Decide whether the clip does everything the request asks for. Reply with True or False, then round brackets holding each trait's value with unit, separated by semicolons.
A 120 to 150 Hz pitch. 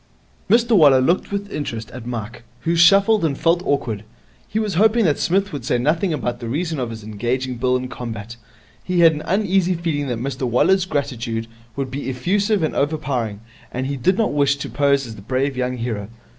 True (140 Hz)